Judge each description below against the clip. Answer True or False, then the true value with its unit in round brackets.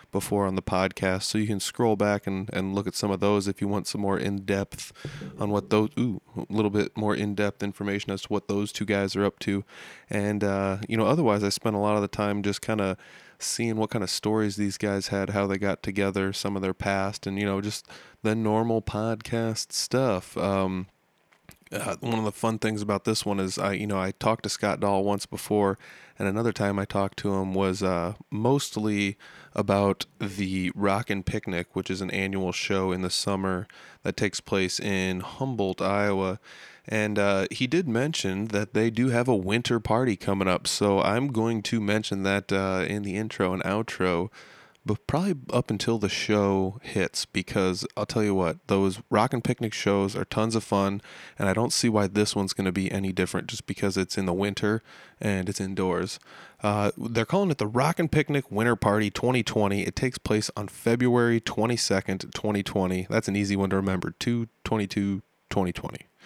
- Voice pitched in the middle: False (100 Hz)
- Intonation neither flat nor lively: False (2.0 semitones)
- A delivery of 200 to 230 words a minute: True (205 wpm)